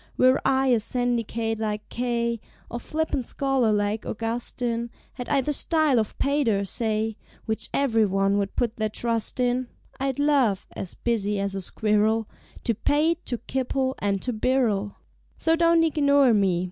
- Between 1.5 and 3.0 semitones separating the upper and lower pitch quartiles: No, average, 3.8 semitones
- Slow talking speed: No, average, 155 wpm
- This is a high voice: Yes, high, 235 Hz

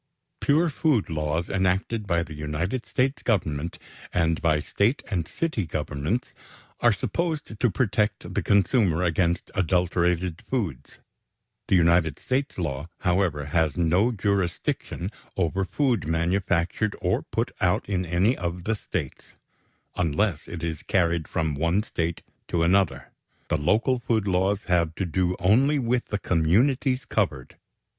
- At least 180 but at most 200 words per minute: No, average, 140 wpm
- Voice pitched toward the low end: Yes, very low, 90 Hz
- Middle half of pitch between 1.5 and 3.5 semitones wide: No, average, 4.6 semitones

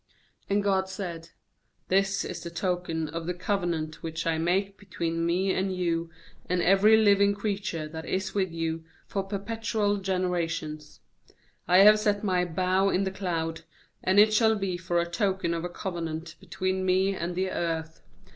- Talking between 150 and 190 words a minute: Yes, average, 165 wpm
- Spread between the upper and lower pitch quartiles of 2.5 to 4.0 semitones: Yes, average, 2.8 semitones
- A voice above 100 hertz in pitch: Yes, medium, 185 Hz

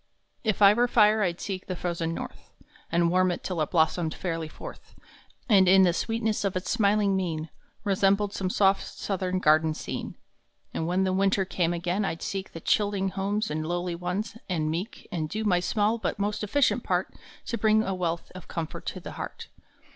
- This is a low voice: No, high, 190 Hz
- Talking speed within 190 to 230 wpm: Yes, average, 200 wpm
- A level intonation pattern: No, average, 3.1 semitones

